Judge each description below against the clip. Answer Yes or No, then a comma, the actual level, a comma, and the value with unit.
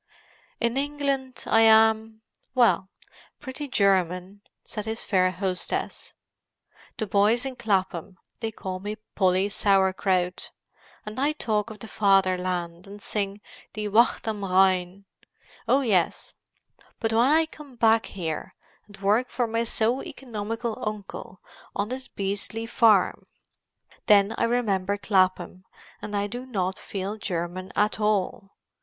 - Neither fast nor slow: No, slow, 130 wpm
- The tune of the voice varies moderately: Yes, average, 3.2 semitones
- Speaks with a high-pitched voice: Yes, high, 210 Hz